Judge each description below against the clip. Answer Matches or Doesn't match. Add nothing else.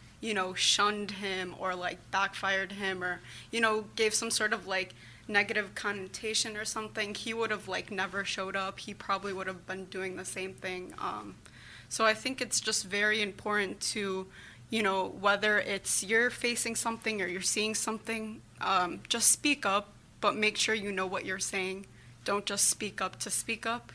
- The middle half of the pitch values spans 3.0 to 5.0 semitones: Doesn't match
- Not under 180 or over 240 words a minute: Matches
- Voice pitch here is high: Matches